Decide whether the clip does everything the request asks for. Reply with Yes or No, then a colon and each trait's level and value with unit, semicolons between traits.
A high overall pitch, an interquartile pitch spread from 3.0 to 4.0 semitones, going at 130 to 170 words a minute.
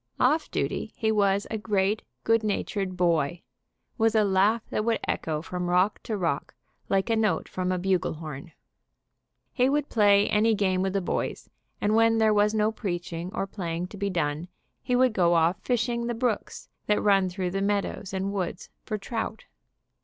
No: high, 200 Hz; average, 3.3 semitones; average, 185 wpm